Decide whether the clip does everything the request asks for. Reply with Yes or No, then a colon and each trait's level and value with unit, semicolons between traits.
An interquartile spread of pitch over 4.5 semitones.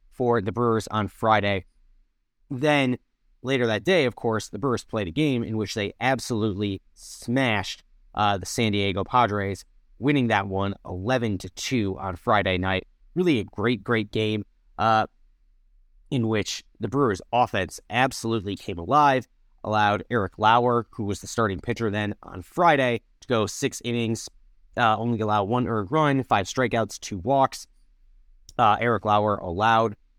No: average, 3.6 semitones